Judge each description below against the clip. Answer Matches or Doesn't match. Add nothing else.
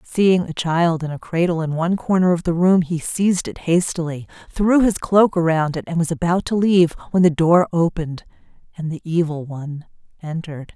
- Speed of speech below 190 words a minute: Doesn't match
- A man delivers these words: Doesn't match